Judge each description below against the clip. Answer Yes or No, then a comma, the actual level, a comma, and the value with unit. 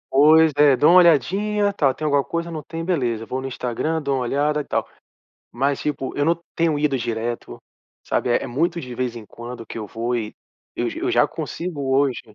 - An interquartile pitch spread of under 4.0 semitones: No, average, 4.6 semitones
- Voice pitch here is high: No, medium, 140 Hz